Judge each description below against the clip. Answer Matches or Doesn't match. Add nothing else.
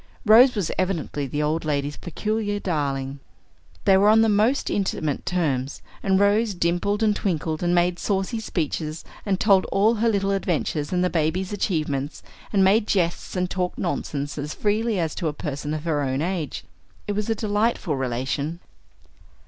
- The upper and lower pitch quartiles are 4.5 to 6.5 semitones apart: Matches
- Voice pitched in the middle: Matches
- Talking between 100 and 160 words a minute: Doesn't match